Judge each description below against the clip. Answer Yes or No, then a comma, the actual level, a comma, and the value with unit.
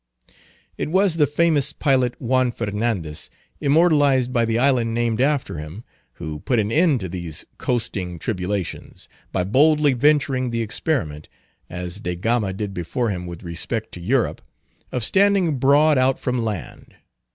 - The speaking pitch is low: Yes, low, 120 Hz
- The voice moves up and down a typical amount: No, wide, 6.6 semitones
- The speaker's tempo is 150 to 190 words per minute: No, average, 140 wpm